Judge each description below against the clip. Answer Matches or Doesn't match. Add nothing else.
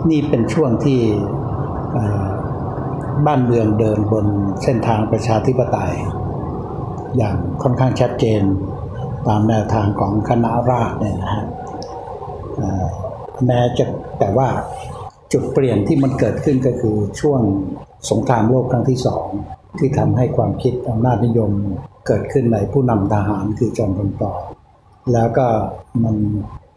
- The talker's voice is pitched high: Doesn't match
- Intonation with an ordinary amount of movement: Matches